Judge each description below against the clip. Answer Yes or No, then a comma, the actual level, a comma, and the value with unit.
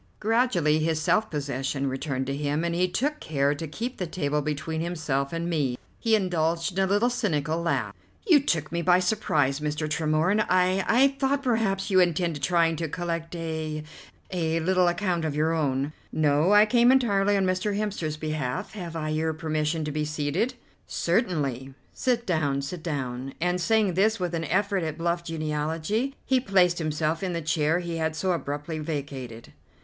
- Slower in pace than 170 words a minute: No, average, 180 wpm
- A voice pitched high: No, medium, 165 Hz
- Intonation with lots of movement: No, average, 3.7 semitones